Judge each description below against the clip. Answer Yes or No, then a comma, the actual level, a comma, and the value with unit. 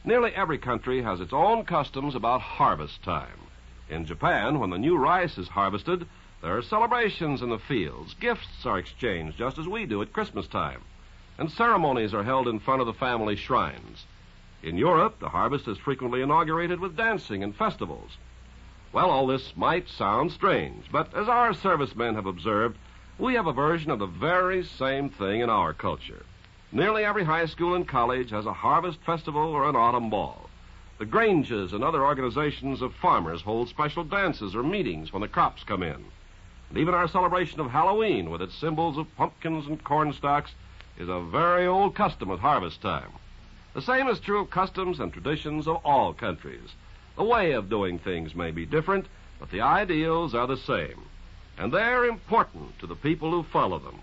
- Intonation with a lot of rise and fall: Yes, wide, 8.8 semitones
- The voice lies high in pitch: No, medium, 145 Hz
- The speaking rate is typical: Yes, average, 185 wpm